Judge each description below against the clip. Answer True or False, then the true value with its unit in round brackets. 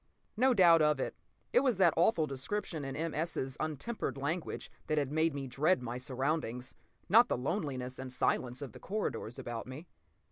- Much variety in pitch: False (4.7 semitones)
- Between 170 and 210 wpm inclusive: True (180 wpm)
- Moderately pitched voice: True (150 Hz)